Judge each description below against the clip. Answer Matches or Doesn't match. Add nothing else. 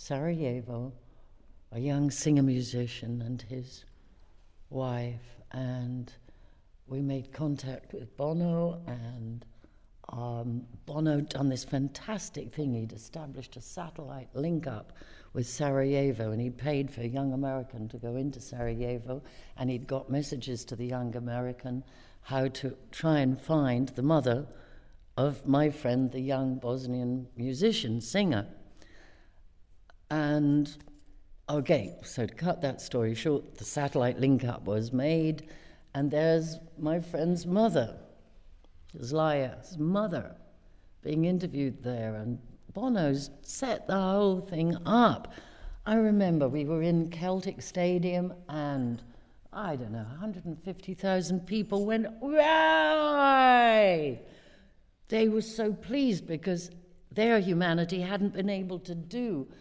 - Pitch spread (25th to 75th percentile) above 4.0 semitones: Matches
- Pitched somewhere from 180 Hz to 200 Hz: Doesn't match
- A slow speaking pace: Matches